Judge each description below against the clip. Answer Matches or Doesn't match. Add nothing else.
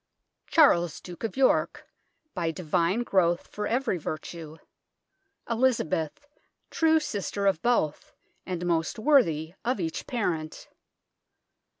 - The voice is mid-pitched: Matches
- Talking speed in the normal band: Doesn't match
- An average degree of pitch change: Doesn't match